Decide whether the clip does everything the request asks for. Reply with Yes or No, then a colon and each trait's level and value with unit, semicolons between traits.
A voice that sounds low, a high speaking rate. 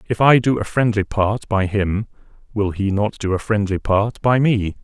Yes: low, 105 Hz; fast, 210 wpm